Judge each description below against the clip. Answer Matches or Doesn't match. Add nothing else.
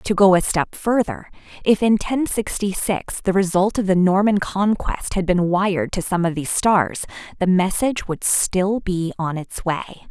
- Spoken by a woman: Matches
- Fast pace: Doesn't match